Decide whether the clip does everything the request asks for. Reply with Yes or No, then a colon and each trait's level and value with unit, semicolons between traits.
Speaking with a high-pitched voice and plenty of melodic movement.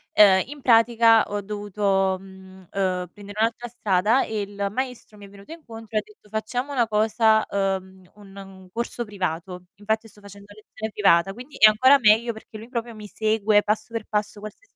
No: high, 210 Hz; narrow, 2.4 semitones